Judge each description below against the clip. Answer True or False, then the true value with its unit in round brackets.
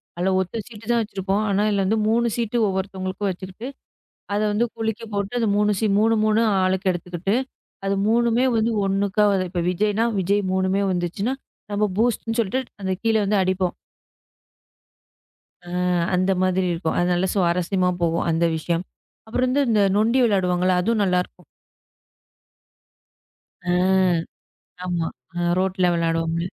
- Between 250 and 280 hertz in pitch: False (195 Hz)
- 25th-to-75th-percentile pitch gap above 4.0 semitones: False (3.2 semitones)